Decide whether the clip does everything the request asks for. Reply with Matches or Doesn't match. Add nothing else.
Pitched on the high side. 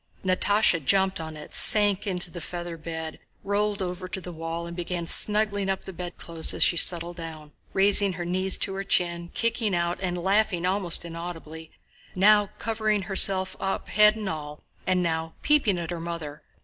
Doesn't match